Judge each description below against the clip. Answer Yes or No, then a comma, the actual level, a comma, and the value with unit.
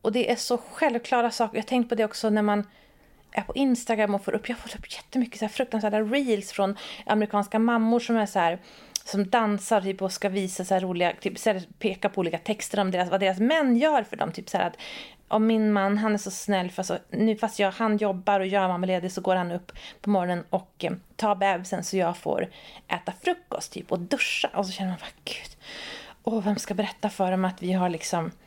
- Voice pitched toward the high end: Yes, high, 205 Hz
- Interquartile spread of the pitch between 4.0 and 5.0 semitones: No, average, 2.9 semitones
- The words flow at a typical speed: No, fast, 235 wpm